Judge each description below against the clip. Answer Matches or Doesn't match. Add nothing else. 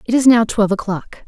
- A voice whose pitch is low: Doesn't match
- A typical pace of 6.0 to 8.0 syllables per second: Matches